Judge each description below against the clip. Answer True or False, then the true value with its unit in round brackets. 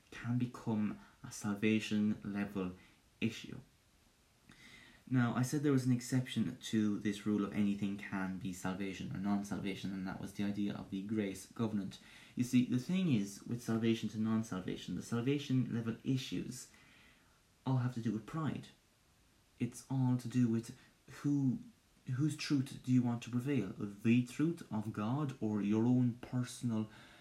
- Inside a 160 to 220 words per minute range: True (165 wpm)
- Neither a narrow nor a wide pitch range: True (3.5 semitones)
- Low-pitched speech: True (115 Hz)